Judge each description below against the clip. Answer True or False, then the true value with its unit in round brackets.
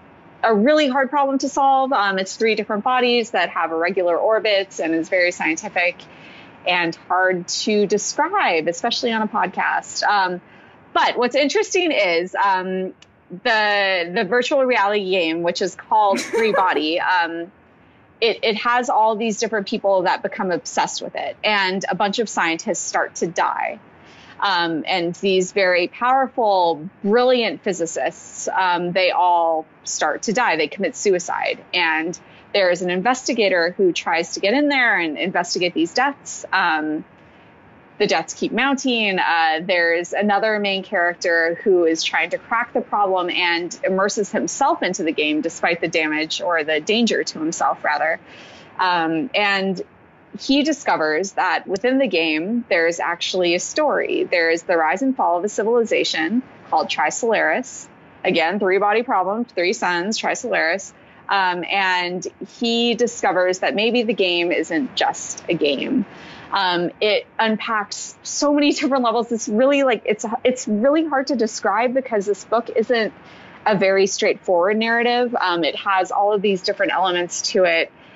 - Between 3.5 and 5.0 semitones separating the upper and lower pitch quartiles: False (5.5 semitones)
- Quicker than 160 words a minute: False (155 wpm)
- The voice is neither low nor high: False (205 Hz)